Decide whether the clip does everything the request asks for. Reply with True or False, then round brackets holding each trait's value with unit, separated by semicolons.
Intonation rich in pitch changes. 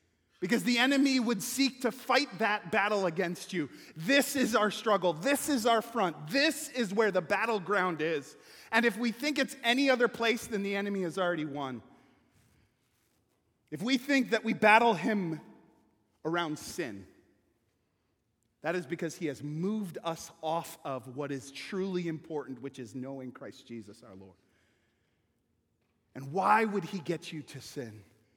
True (8.8 semitones)